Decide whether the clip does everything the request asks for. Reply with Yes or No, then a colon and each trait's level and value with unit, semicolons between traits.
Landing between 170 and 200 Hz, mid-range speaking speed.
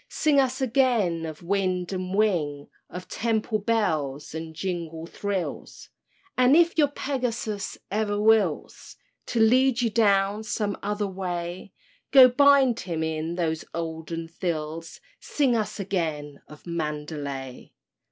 No: high, 190 Hz; slow, 125 wpm